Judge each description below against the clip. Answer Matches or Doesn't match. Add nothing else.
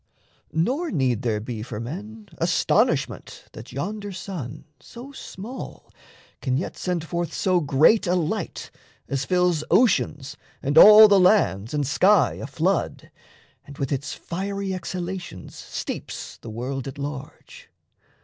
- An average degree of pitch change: Doesn't match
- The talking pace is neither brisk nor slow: Doesn't match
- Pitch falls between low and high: Matches